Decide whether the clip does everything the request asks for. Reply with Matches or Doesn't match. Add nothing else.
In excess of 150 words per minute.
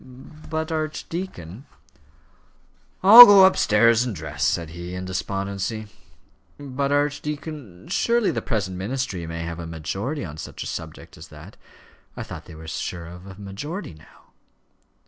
Doesn't match